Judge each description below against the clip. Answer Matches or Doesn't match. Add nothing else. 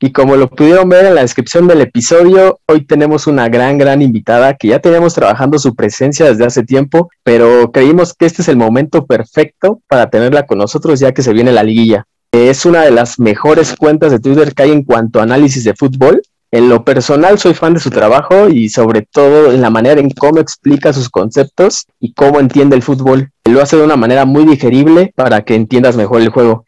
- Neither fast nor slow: Doesn't match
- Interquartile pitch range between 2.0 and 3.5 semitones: Doesn't match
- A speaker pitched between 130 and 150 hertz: Matches